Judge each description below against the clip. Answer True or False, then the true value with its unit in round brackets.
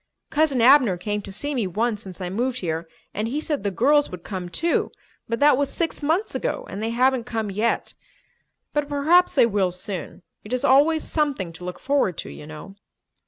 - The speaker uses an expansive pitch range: True (7.0 semitones)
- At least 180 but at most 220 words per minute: True (205 wpm)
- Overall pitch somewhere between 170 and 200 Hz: False (235 Hz)